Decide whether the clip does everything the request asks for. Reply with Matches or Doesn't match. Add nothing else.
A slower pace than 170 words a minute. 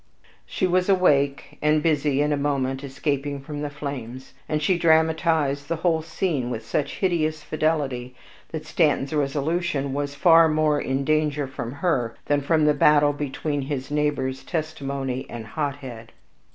Matches